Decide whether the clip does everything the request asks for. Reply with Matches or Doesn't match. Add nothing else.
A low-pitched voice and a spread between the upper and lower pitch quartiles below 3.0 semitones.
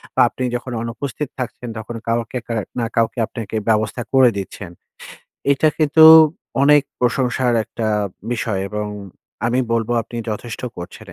Matches